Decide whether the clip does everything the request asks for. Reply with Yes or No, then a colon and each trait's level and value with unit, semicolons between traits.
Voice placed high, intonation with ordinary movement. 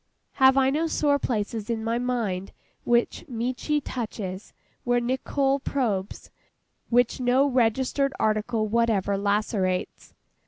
Yes: high, 235 Hz; average, 3.7 semitones